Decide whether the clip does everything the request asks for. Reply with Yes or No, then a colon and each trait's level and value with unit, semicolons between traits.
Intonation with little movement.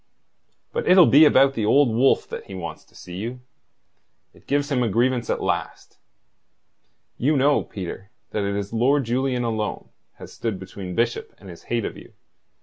No: average, 5.1 semitones